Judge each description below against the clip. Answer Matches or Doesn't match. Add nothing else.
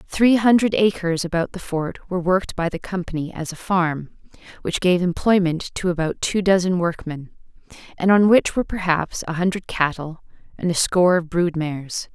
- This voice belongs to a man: Doesn't match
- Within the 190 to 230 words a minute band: Doesn't match